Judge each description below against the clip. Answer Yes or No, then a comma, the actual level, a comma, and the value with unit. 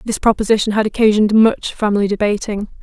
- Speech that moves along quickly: No, average, 150 wpm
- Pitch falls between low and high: No, high, 210 Hz